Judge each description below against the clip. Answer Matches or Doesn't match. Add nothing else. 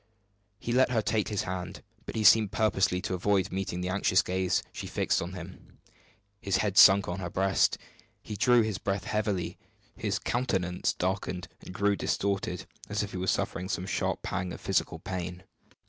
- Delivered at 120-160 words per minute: Doesn't match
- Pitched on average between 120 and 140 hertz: Doesn't match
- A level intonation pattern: Matches